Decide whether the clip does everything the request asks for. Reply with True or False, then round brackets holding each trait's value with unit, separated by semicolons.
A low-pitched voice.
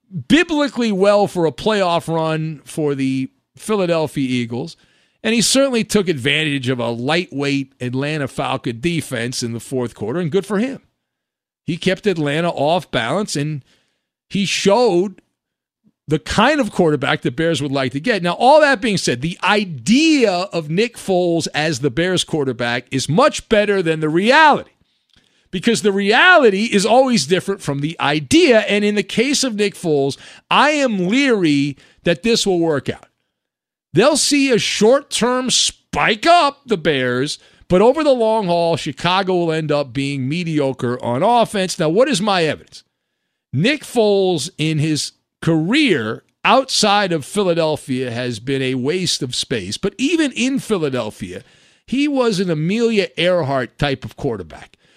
False (175 Hz)